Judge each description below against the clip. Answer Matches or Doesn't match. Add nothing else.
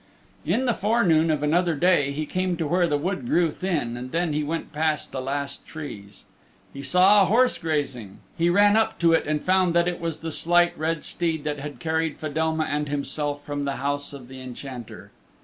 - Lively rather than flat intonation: Doesn't match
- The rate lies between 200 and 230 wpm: Matches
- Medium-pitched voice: Matches